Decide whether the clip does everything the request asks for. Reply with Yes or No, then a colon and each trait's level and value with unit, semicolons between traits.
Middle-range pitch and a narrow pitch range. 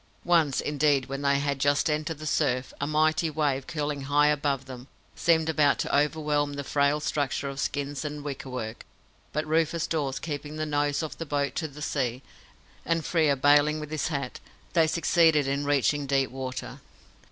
Yes: medium, 145 Hz; narrow, 1.8 semitones